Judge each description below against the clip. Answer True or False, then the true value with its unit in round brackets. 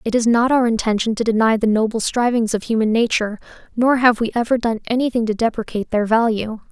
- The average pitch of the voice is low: False (225 Hz)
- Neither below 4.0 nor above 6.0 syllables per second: False (6.2 syllables/s)